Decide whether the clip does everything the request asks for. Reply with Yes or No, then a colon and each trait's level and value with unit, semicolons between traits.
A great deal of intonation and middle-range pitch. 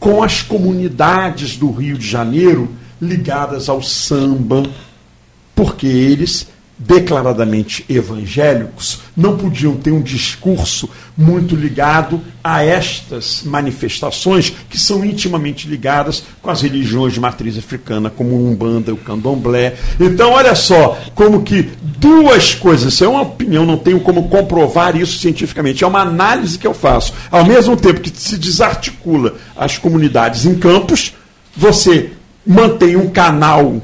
Yes: wide, 5.7 semitones; medium, 155 Hz